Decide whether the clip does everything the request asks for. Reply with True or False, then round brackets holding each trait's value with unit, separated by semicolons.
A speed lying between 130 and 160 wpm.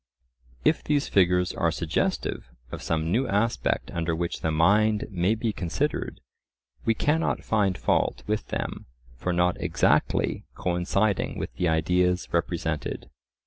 True (135 wpm)